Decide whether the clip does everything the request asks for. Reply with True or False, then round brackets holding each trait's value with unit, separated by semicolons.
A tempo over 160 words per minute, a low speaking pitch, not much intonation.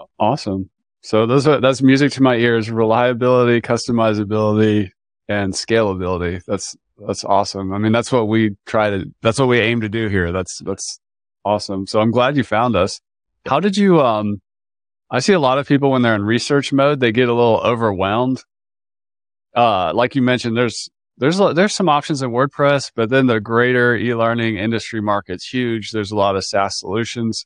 False (185 wpm; 115 Hz; 3.5 semitones)